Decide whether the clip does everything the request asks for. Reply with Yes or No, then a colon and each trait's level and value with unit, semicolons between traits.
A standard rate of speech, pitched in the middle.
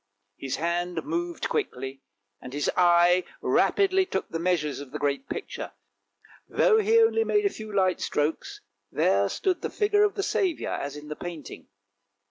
Yes: average, 165 wpm; medium, 180 Hz